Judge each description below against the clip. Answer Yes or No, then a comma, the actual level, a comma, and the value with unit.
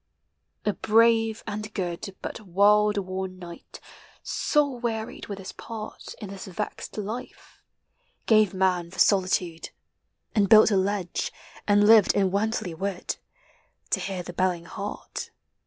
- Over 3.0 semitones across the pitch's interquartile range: No, average, 2.7 semitones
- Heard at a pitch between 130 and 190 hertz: No, high, 200 Hz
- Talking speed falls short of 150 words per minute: Yes, average, 140 wpm